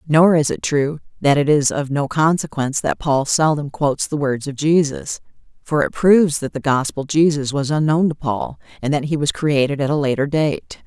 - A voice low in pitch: No, medium, 145 Hz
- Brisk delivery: Yes, fast, 210 wpm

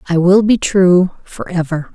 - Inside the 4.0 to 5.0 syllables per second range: Yes, 4.2 syllables/s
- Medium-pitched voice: Yes, medium, 180 Hz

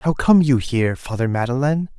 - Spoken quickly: No, average, 180 wpm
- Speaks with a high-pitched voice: No, low, 135 Hz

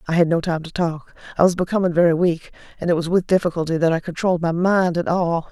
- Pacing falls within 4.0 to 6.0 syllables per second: No, 6.4 syllables/s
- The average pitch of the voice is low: No, medium, 170 Hz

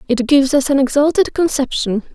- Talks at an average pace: Yes, average, 170 wpm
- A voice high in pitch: Yes, very high, 275 Hz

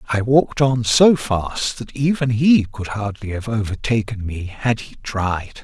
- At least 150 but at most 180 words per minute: Yes, average, 170 wpm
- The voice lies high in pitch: No, low, 115 Hz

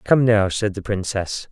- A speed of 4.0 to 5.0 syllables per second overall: Yes, 4.3 syllables/s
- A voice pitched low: Yes, low, 105 Hz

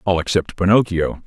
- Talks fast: No, average, 145 wpm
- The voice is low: Yes, very low, 95 Hz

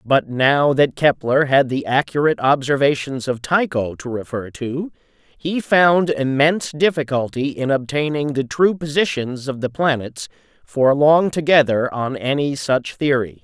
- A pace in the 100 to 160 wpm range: Yes, average, 145 wpm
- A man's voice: Yes, male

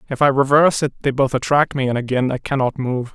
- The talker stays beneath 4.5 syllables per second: No, 6.2 syllables/s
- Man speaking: Yes, male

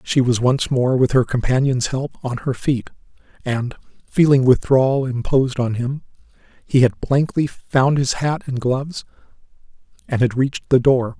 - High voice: No, low, 130 Hz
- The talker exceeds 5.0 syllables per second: No, 4.7 syllables/s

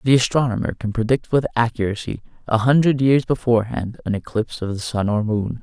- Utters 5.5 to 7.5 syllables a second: Yes, 5.9 syllables/s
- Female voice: No, male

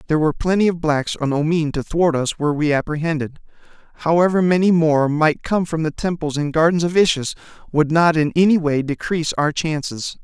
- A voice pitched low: No, medium, 160 Hz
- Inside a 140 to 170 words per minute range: No, average, 195 wpm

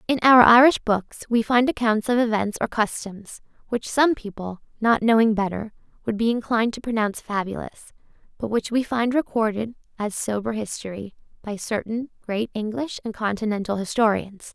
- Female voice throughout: Yes, female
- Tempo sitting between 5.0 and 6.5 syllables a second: Yes, 5.1 syllables/s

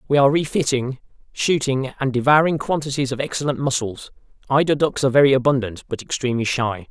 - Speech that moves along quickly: No, average, 155 wpm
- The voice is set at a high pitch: No, low, 135 Hz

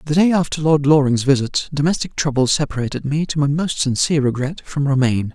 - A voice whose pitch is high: No, medium, 145 Hz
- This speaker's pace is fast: No, average, 190 wpm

